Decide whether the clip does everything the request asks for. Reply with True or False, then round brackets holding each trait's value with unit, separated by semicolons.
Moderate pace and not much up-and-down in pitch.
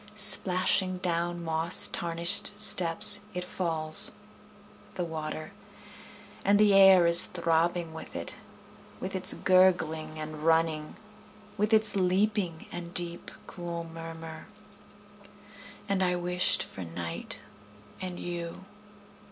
False (110 wpm; 2.2 semitones)